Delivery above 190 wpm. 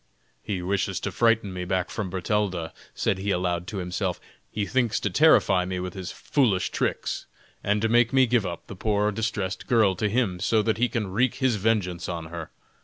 Yes: average, 200 wpm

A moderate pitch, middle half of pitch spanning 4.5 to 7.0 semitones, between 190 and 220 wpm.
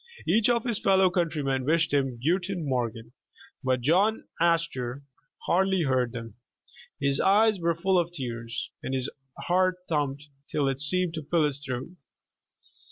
No: medium, 155 Hz; wide, 5.6 semitones; average, 150 wpm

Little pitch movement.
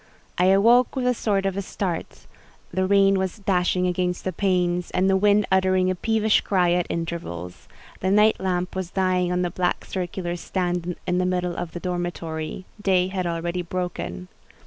Yes: narrow, 1.5 semitones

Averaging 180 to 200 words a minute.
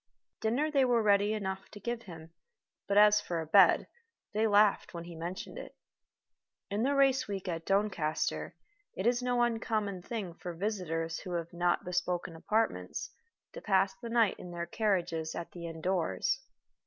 No: average, 170 wpm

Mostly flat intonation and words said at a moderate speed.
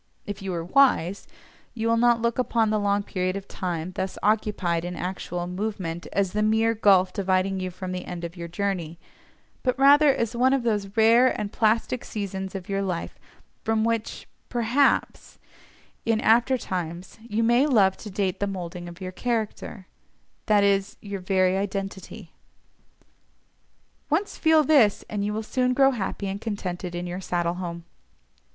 No: average, 3.7 semitones; average, 165 wpm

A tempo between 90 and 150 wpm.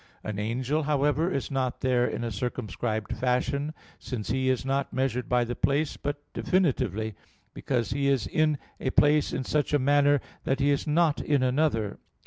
No: average, 175 wpm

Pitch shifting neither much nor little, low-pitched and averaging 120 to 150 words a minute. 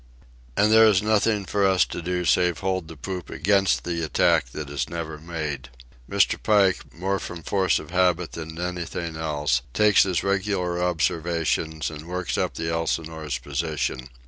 No: average, 3.0 semitones; very low, 85 Hz; average, 165 wpm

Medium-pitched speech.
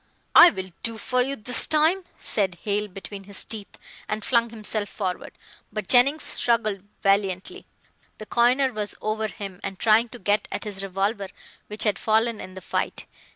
No: high, 215 Hz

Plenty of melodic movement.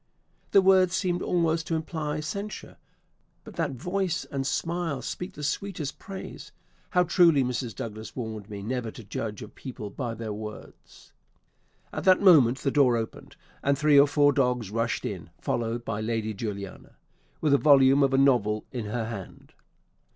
Yes: wide, 6.0 semitones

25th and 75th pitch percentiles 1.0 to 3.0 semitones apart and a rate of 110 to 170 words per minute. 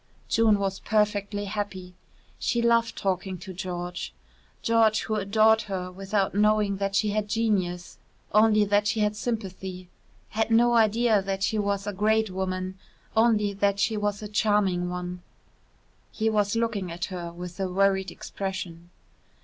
Yes: narrow, 2.4 semitones; average, 150 wpm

